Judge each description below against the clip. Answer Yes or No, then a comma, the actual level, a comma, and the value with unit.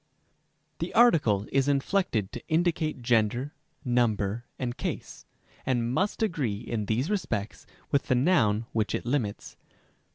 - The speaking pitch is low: Yes, low, 120 Hz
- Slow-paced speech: Yes, slow, 130 wpm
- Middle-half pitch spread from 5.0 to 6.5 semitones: Yes, wide, 5.6 semitones